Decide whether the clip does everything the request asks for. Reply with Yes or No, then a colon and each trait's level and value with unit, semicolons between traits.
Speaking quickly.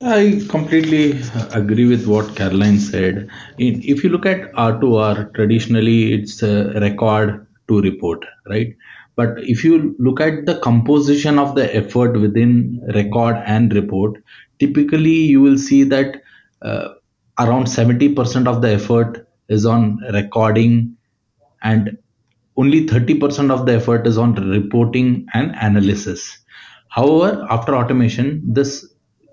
No: slow, 135 wpm